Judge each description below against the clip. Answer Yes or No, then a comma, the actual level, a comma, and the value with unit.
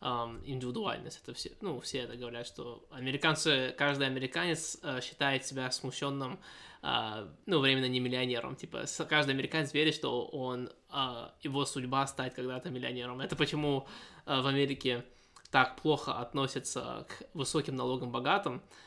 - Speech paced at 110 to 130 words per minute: Yes, average, 125 wpm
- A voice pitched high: No, low, 135 Hz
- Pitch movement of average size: No, narrow, 2.1 semitones